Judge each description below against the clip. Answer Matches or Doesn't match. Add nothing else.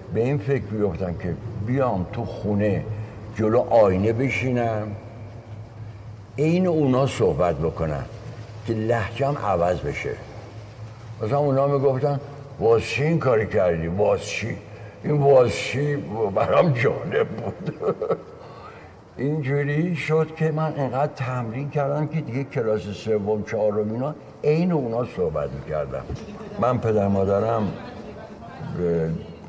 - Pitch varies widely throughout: Doesn't match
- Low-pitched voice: Matches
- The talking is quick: Doesn't match